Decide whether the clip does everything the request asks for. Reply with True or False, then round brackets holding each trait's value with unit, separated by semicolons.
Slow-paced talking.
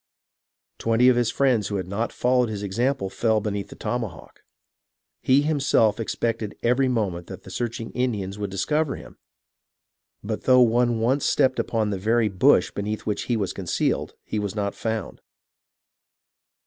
False (160 wpm)